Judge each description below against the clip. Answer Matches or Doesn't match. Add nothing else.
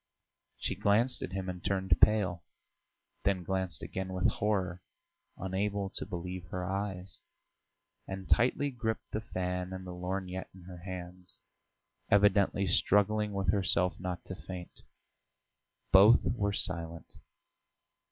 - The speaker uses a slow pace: Matches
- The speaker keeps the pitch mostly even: Matches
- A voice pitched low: Matches